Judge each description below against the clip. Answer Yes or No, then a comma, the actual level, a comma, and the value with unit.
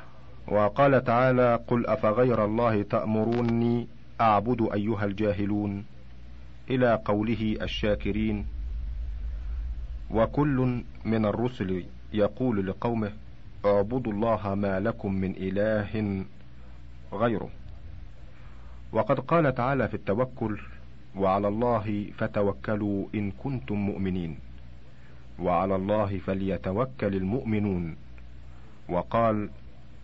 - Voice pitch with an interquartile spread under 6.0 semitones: No, wide, 7.4 semitones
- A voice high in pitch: No, low, 100 Hz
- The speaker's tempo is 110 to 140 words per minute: No, average, 80 wpm